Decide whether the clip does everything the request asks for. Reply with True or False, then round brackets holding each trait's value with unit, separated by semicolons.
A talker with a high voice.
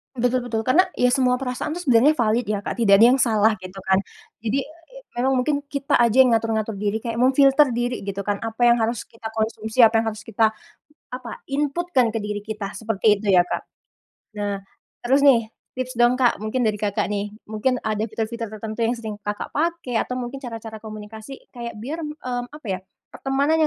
True (230 Hz)